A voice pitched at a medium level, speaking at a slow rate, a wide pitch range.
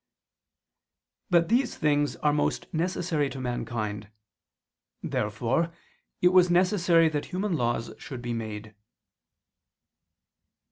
Yes: medium, 150 Hz; slow, 100 wpm; wide, 6.8 semitones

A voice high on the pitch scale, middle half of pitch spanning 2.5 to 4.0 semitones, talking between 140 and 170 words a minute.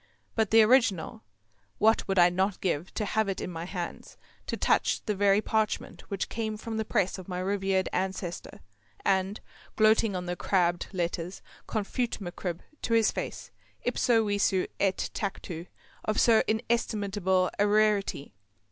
Yes: high, 195 Hz; average, 2.9 semitones; average, 155 wpm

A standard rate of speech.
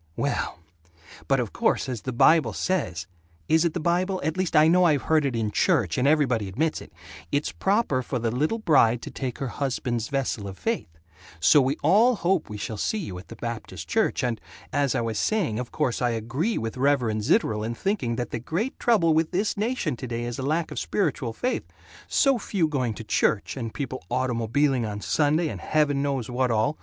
No: fast, 210 wpm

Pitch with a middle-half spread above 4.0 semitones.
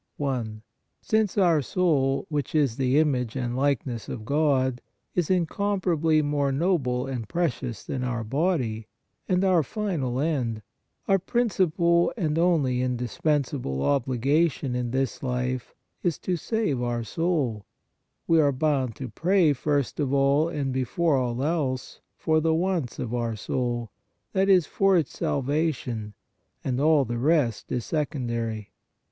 Yes: average, 4.8 semitones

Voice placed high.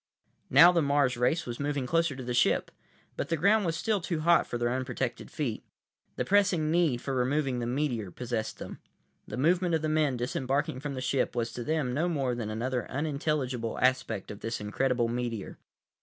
No: low, 130 Hz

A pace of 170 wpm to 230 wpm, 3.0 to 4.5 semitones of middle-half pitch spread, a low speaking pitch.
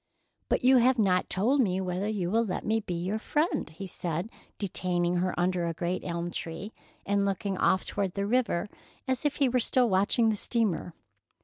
No: average, 195 wpm; average, 4.2 semitones; high, 195 Hz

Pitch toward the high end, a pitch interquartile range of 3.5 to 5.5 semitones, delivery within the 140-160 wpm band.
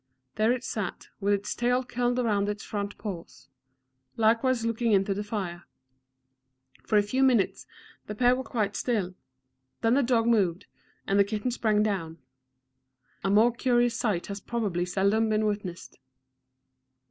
No: high, 215 Hz; average, 3.0 semitones; average, 150 wpm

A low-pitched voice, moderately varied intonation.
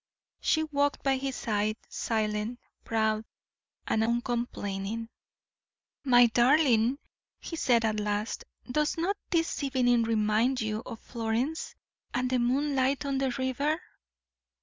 No: high, 245 Hz; average, 3.7 semitones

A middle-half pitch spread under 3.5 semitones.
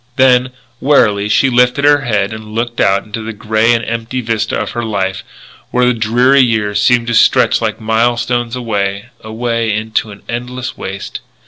Yes: narrow, 2.4 semitones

